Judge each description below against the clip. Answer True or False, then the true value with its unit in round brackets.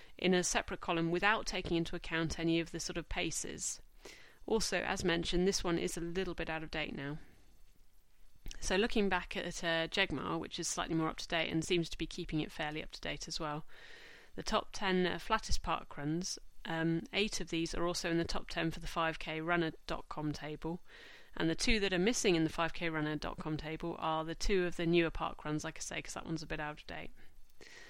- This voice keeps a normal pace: False (220 wpm)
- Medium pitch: True (165 Hz)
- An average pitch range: False (2.3 semitones)